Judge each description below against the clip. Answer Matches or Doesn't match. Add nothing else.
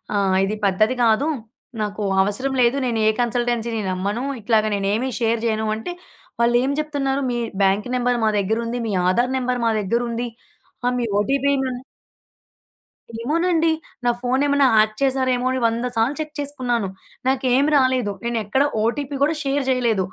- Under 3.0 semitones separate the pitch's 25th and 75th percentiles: Doesn't match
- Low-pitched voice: Doesn't match